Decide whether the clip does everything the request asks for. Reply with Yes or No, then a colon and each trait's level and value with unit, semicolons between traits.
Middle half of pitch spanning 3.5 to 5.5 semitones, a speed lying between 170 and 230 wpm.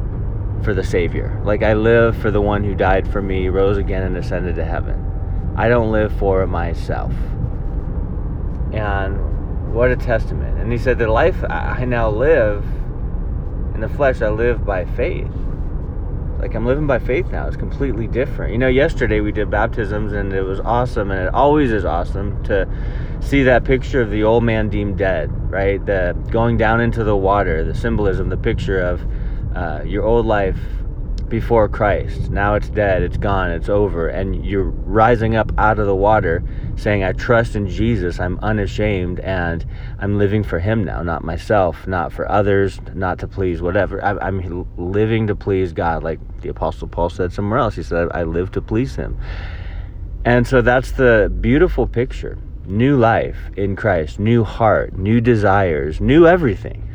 Yes: average, 3.8 semitones; average, 175 wpm